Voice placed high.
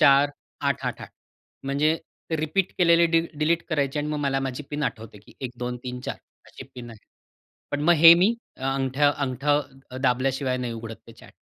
No: medium, 140 Hz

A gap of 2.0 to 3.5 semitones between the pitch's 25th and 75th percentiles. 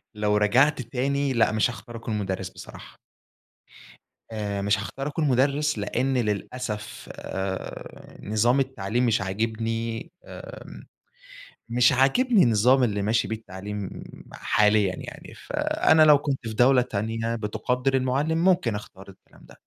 No: average, 4.2 semitones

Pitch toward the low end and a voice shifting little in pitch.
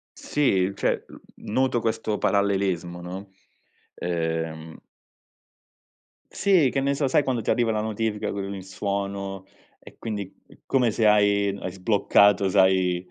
No: low, 100 Hz; average, 3.1 semitones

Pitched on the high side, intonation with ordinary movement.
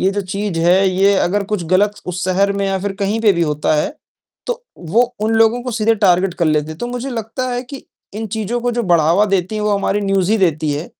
Yes: high, 200 Hz; average, 3.7 semitones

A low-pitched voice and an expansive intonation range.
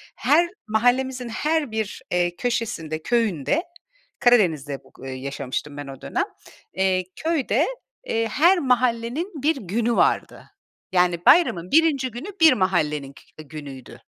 No: high, 220 Hz; wide, 8.7 semitones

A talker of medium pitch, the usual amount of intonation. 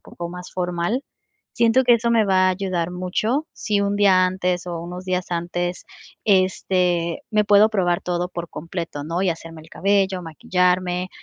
No: medium, 180 Hz; narrow, 2.3 semitones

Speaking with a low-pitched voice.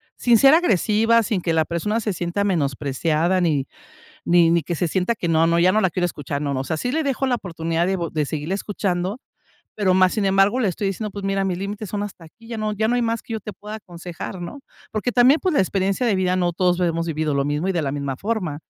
No: medium, 185 Hz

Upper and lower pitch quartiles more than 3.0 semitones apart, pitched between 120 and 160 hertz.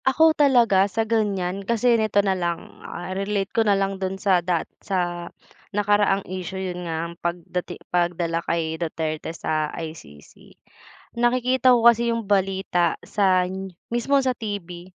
No: average, 3.9 semitones; high, 190 Hz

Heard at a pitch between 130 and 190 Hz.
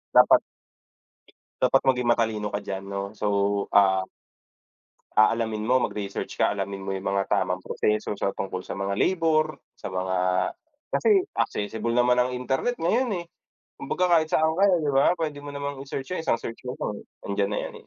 No: low, 115 Hz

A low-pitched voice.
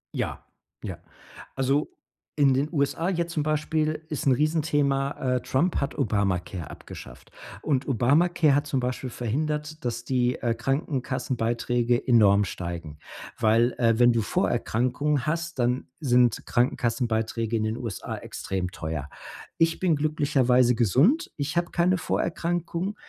Yes: low, 130 Hz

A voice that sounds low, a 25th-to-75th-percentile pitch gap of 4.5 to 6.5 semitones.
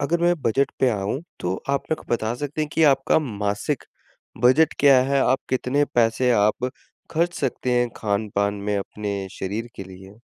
Yes: low, 120 Hz; average, 5.2 semitones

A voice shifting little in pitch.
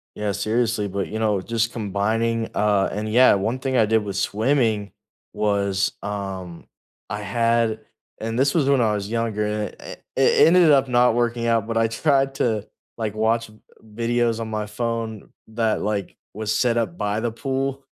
Yes: narrow, 2.2 semitones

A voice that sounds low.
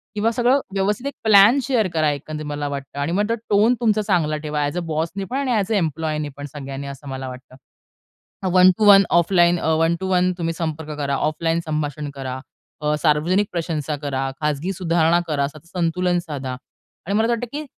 No: medium, 165 Hz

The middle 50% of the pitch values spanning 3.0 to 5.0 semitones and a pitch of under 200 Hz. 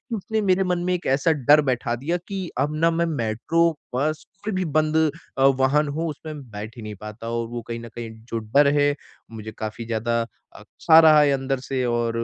No: wide, 5.4 semitones; low, 135 Hz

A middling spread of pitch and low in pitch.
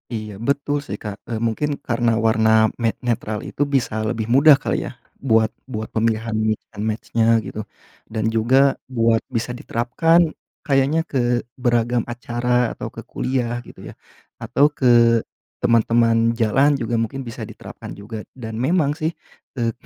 Yes: average, 3.0 semitones; low, 120 Hz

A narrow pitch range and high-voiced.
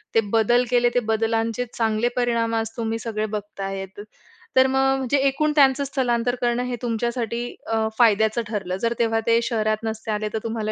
Yes: narrow, 1.9 semitones; high, 230 Hz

